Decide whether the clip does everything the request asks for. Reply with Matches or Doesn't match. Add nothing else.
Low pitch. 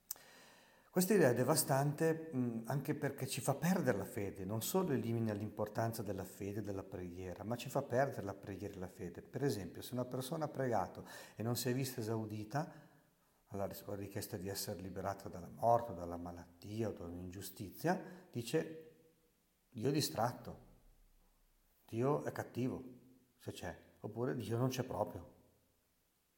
Matches